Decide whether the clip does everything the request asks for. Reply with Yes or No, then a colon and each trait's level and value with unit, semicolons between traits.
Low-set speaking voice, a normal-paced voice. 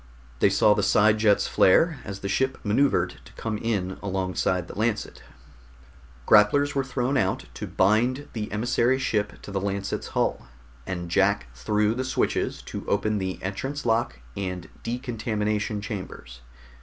Yes: low, 105 Hz; average, 150 wpm